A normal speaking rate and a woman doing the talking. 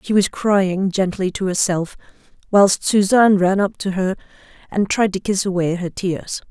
Yes: average, 175 wpm; female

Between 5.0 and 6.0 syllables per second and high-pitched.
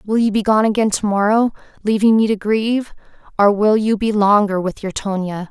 Yes: 5.4 syllables/s; high, 210 Hz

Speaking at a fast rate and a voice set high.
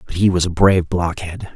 No: fast, 230 wpm; very low, 90 Hz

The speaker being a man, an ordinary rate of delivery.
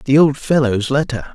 Yes: male; average, 180 wpm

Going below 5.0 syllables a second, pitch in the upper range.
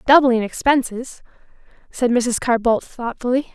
Yes: 4.4 syllables/s; high, 245 Hz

